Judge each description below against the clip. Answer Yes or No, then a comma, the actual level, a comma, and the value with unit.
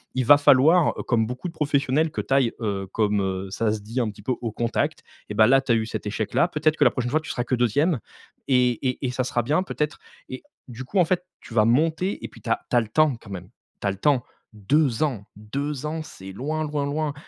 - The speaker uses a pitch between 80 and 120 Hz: No, low, 130 Hz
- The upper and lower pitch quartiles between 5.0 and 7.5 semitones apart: Yes, average, 5.3 semitones